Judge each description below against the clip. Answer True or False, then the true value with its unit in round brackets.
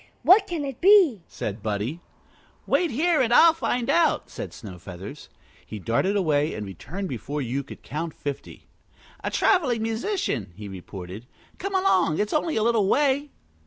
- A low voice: False (195 Hz)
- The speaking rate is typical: True (160 wpm)